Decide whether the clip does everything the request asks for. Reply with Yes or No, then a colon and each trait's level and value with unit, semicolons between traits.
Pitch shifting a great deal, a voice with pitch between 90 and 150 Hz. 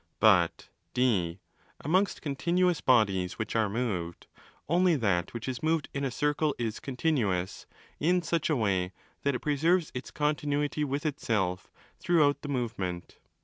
Yes: wide, 6.6 semitones; low, 135 Hz